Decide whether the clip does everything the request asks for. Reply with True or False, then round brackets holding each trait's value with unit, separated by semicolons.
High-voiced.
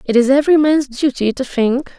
True (270 Hz)